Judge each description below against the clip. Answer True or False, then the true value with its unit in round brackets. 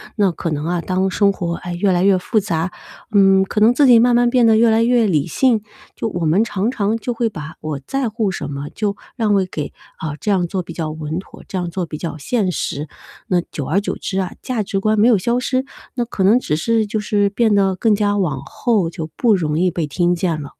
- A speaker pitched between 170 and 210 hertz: True (195 Hz)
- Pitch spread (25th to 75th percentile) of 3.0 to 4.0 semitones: False (4.6 semitones)